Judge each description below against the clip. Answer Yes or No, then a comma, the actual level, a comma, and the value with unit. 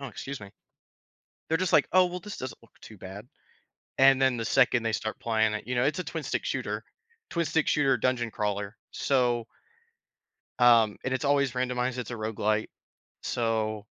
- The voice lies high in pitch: No, low, 120 Hz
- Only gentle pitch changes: No, average, 3.6 semitones